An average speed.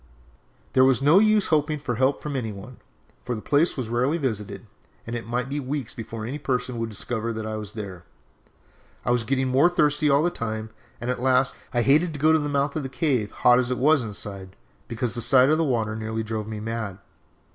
No: fast, 225 wpm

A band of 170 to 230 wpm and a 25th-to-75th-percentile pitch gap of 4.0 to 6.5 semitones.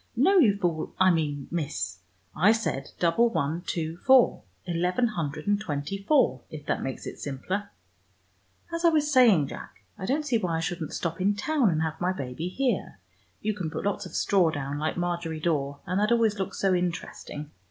Yes: average, 195 wpm; average, 5.1 semitones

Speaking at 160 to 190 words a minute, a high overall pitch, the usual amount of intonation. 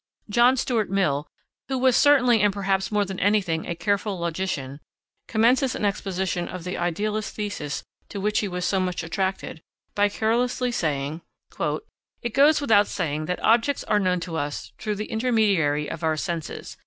Yes: average, 165 wpm; high, 195 Hz; average, 4.4 semitones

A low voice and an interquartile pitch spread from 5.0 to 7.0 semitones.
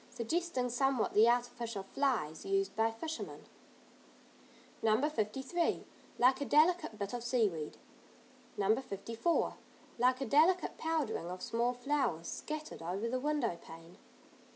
No: high, 245 Hz; wide, 5.5 semitones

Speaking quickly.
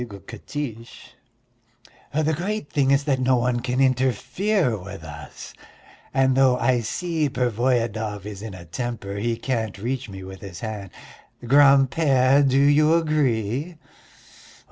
No: average, 140 wpm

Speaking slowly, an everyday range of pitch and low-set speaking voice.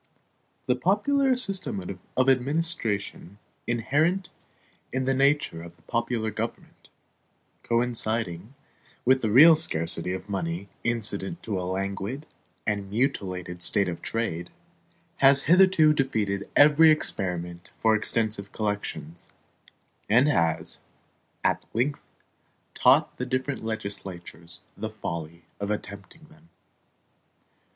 No: slow, 105 wpm; wide, 6.2 semitones; low, 110 Hz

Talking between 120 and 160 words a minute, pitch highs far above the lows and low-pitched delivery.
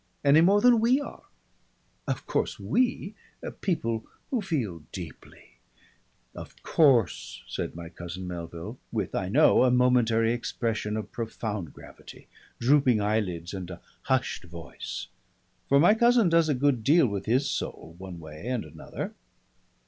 Yes: average, 145 wpm; wide, 8.3 semitones; low, 115 Hz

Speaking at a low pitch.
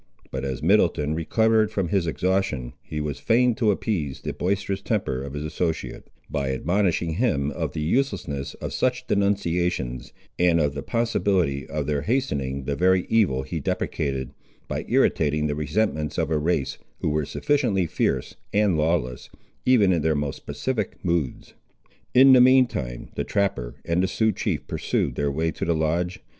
Yes: very low, 80 Hz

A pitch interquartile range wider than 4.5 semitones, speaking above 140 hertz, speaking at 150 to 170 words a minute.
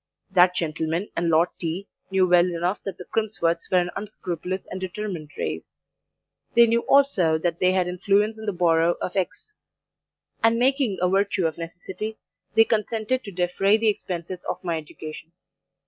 No: average, 3.6 semitones; medium, 185 Hz; average, 165 wpm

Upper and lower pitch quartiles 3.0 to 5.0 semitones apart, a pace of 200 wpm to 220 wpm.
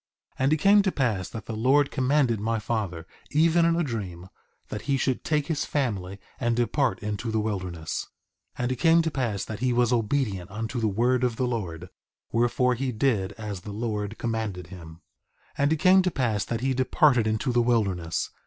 Yes: average, 4.5 semitones; fast, 205 wpm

